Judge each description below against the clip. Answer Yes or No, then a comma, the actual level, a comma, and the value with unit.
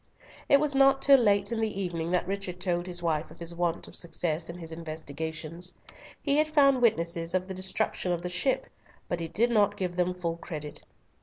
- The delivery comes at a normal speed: No, fast, 210 wpm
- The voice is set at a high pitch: No, medium, 180 Hz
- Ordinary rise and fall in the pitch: Yes, average, 3.6 semitones